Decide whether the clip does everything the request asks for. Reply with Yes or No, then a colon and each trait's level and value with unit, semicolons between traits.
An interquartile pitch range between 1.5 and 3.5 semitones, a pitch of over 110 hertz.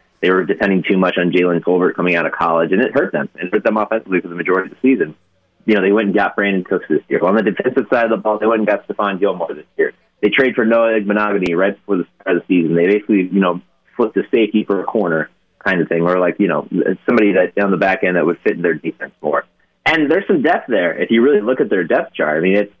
No: average, 2.9 semitones; low, 100 Hz